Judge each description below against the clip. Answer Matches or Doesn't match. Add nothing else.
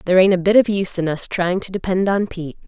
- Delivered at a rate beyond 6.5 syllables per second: Matches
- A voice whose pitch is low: Doesn't match